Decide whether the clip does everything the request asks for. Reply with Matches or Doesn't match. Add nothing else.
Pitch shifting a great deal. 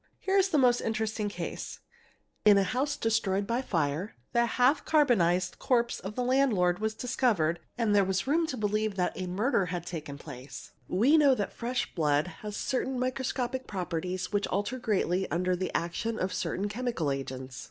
Matches